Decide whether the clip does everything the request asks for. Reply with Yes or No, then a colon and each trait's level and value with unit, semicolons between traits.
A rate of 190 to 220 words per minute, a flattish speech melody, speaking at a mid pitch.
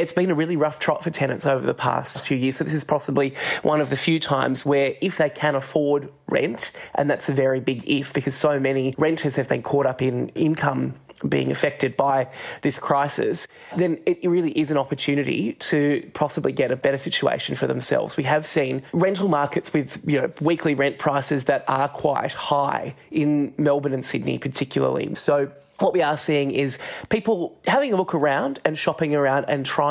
Yes: average, 200 wpm; narrow, 2.3 semitones; medium, 145 Hz